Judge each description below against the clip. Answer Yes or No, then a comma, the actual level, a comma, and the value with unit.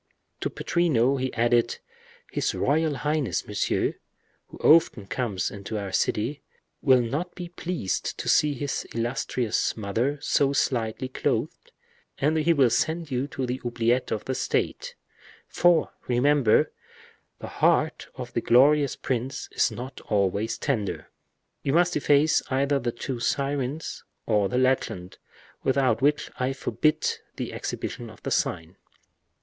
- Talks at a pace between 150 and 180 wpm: No, average, 140 wpm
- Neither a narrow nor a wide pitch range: Yes, average, 4.0 semitones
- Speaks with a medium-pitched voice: No, low, 130 Hz